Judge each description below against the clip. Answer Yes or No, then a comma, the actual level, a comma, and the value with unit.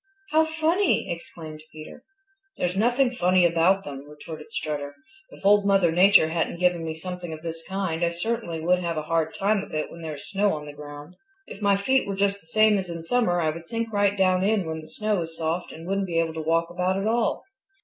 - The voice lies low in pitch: No, medium, 175 Hz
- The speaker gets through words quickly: Yes, fast, 230 wpm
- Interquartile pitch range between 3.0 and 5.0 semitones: Yes, average, 3.8 semitones